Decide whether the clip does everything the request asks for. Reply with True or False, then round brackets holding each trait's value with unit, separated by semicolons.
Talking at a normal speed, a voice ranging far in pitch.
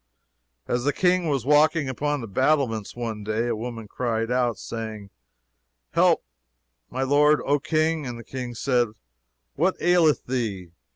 False (150 wpm; 4.5 semitones)